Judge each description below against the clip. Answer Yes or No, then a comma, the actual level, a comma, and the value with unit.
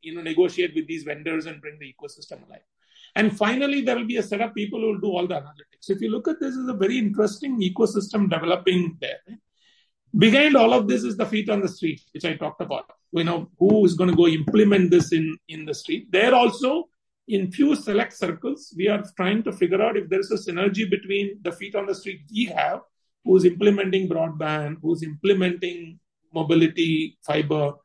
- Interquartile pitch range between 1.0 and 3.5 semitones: No, average, 4.8 semitones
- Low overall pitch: No, high, 200 Hz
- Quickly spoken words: Yes, fast, 215 wpm